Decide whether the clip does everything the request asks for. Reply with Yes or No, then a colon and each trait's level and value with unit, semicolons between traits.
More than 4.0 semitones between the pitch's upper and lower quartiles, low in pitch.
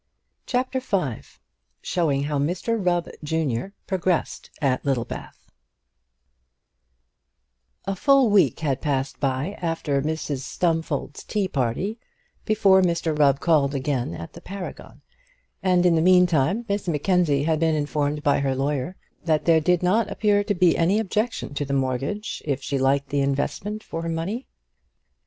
No: average, 5.2 semitones; medium, 165 Hz